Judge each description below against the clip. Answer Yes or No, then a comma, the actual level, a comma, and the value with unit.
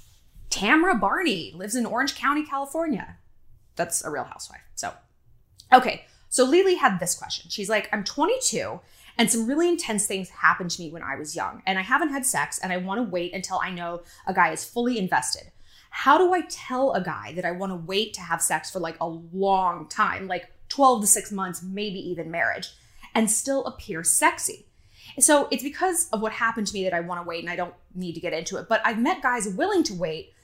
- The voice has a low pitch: No, high, 205 Hz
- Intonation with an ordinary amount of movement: No, wide, 7.4 semitones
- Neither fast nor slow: No, fast, 220 wpm